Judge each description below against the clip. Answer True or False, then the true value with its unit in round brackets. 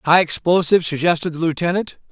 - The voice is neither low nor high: True (170 Hz)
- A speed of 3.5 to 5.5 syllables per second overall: False (6.4 syllables/s)